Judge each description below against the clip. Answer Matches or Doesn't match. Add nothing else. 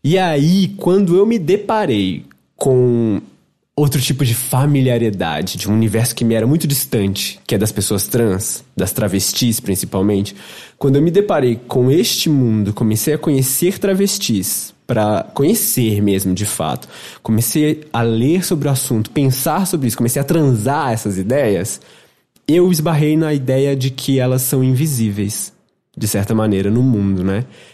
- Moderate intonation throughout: Doesn't match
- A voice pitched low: Matches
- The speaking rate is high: Doesn't match